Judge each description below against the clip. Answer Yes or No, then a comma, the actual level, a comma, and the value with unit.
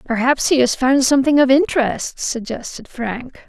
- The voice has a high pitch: Yes, very high, 260 Hz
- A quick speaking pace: No, average, 155 wpm